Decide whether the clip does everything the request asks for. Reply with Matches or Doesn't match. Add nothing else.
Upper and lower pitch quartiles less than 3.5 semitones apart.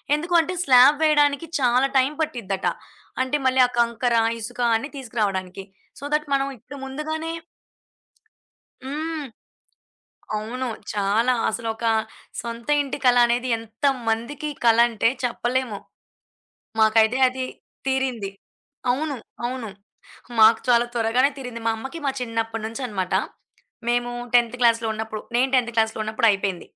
Matches